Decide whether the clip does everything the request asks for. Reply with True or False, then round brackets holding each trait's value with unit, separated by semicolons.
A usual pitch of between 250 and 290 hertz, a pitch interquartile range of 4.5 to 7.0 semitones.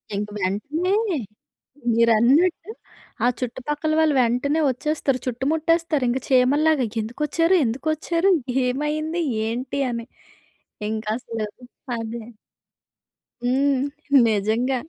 True (265 Hz; 4.9 semitones)